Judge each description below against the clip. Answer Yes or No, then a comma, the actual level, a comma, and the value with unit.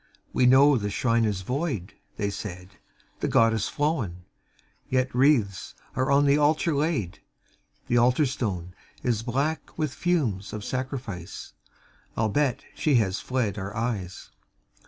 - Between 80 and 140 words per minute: Yes, slow, 135 wpm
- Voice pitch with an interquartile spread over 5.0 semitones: Yes, wide, 5.6 semitones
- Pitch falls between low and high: No, low, 120 Hz